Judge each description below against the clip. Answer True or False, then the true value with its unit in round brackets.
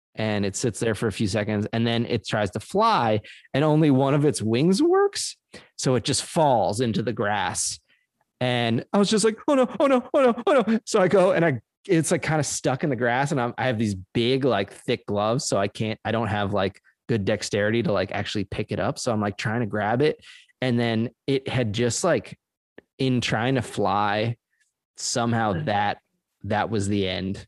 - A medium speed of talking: False (215 wpm)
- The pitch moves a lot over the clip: True (5.8 semitones)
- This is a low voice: True (120 Hz)